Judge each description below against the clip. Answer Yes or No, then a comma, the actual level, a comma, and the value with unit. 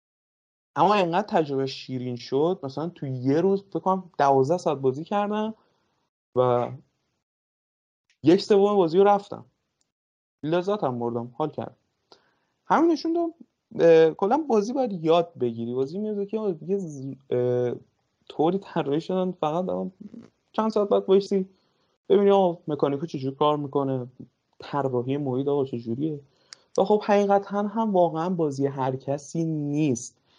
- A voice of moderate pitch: Yes, medium, 165 Hz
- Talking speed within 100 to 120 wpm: No, average, 135 wpm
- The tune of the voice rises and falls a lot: Yes, wide, 6.6 semitones